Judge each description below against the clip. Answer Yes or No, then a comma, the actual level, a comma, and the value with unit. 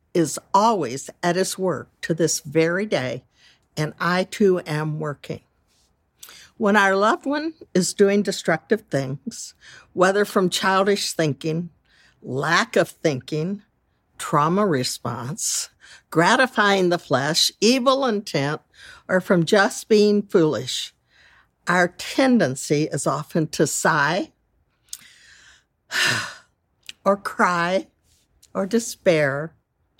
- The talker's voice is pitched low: No, medium, 180 Hz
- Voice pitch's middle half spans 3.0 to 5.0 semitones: Yes, average, 4.7 semitones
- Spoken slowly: Yes, slow, 100 wpm